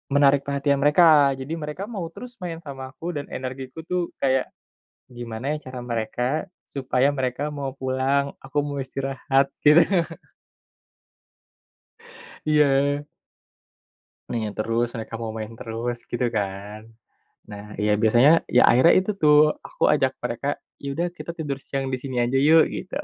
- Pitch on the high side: No, low, 135 Hz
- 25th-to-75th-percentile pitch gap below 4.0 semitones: Yes, average, 3.5 semitones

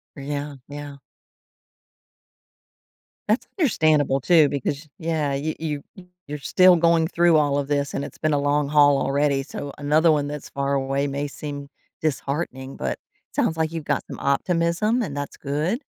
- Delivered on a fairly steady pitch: Yes, narrow, 2.3 semitones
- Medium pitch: Yes, medium, 145 Hz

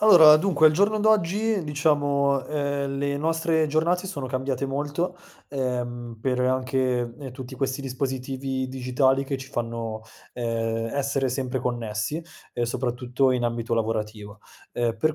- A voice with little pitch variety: No, average, 3.2 semitones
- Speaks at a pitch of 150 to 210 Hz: No, low, 135 Hz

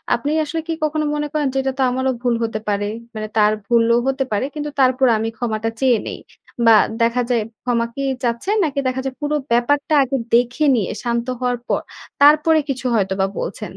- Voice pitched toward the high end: Yes, very high, 250 Hz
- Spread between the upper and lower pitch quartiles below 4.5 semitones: Yes, average, 3.5 semitones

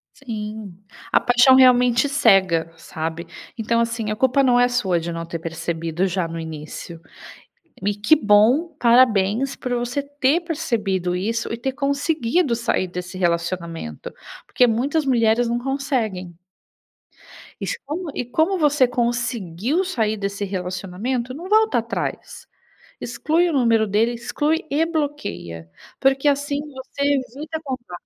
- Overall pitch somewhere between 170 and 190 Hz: No, high, 235 Hz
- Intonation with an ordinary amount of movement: No, wide, 6.6 semitones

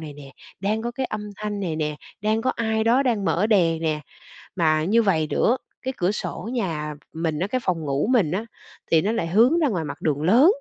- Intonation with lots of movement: Yes, wide, 6.1 semitones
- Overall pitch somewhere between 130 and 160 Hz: No, high, 195 Hz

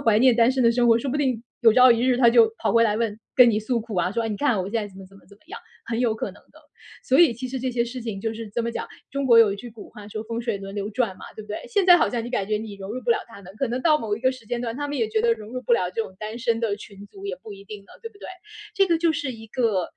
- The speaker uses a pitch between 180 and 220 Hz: No, high, 230 Hz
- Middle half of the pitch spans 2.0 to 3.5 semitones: Yes, average, 3.1 semitones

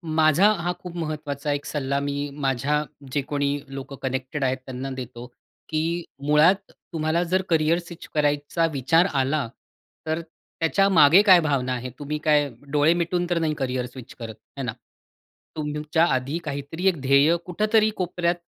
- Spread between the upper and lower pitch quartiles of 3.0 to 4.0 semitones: Yes, average, 3.4 semitones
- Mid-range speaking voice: Yes, medium, 150 Hz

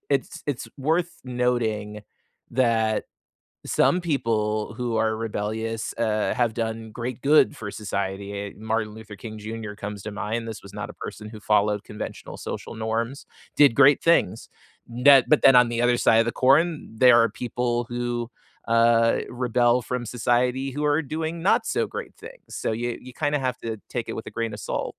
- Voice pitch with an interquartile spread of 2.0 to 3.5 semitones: Yes, narrow, 2.6 semitones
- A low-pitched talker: Yes, low, 115 Hz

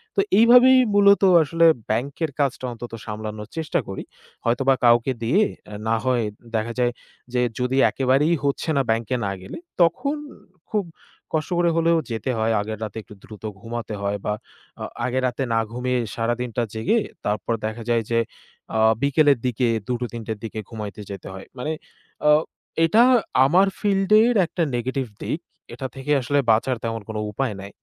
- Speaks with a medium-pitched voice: No, low, 125 Hz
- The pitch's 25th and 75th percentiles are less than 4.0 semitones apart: No, average, 5.3 semitones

